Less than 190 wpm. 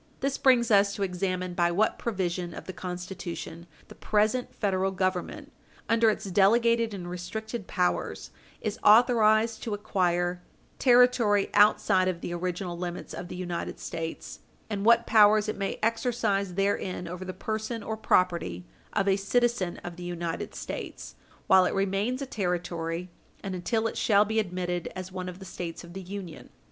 Yes: average, 165 wpm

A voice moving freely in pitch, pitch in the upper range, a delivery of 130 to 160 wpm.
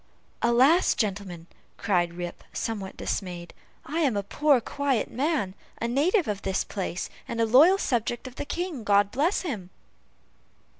Yes: wide, 6.6 semitones; high, 230 Hz; average, 150 wpm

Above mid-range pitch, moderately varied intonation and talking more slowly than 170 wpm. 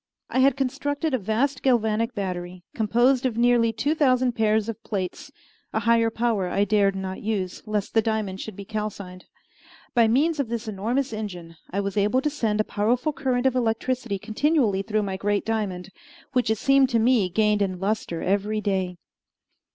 No: high, 220 Hz; average, 3.7 semitones; average, 180 wpm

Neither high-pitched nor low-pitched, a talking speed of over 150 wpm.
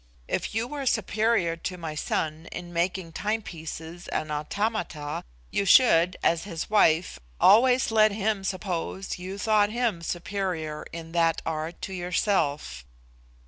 No: medium, 180 Hz; slow, 135 wpm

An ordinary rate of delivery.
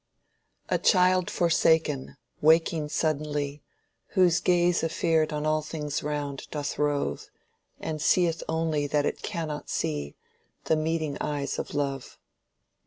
No: slow, 120 wpm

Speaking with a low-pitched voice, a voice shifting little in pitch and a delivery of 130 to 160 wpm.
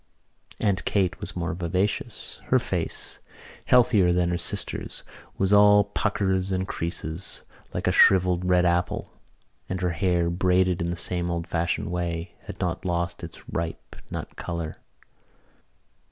Yes: very low, 90 Hz; narrow, 1.6 semitones; average, 140 wpm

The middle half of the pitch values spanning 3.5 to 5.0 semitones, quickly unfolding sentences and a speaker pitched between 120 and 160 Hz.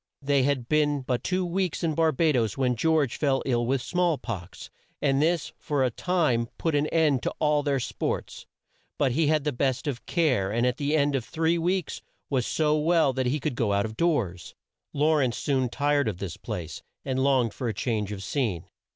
Yes: average, 4.2 semitones; fast, 210 wpm; medium, 140 Hz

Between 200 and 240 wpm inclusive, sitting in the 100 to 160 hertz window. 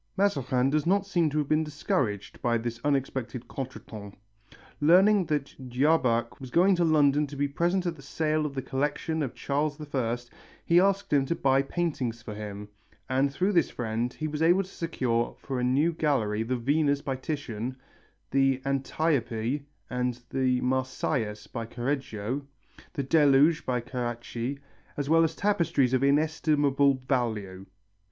No: average, 155 wpm; medium, 140 Hz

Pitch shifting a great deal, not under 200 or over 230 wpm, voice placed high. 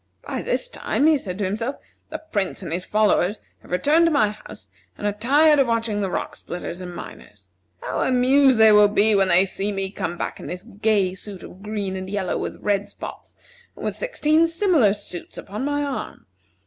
Yes: wide, 6.1 semitones; fast, 205 wpm; high, 210 Hz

